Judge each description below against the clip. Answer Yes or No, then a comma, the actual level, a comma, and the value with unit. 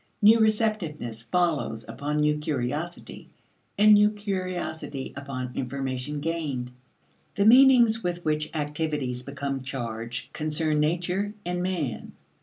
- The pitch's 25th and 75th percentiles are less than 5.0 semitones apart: No, average, 5.3 semitones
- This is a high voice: No, medium, 150 Hz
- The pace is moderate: No, slow, 110 wpm